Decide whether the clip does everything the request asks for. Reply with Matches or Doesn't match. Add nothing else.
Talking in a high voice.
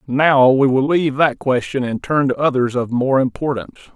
Doesn't match